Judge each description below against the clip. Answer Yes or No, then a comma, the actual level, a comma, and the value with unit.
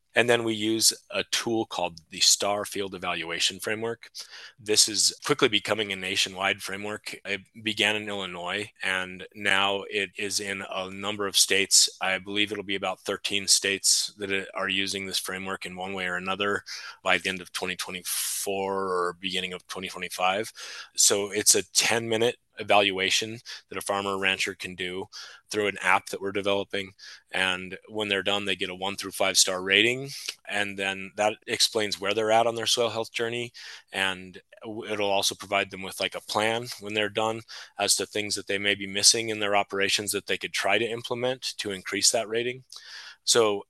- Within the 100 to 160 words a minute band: No, average, 185 wpm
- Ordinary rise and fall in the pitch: No, narrow, 1.9 semitones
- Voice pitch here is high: No, low, 100 Hz